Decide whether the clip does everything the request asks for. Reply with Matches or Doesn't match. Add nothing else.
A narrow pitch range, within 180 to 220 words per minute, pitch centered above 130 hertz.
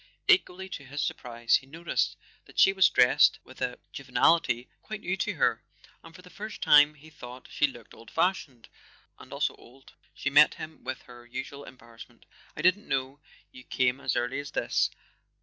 Doesn't match